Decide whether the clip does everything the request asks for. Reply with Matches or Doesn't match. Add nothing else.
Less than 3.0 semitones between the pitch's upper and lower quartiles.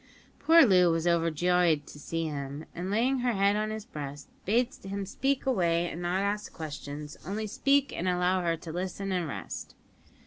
Doesn't match